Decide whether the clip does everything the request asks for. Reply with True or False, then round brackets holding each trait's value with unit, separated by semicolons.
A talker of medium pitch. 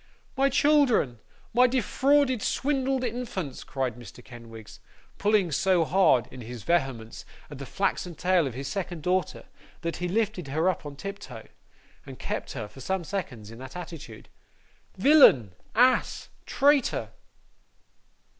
True (180 Hz)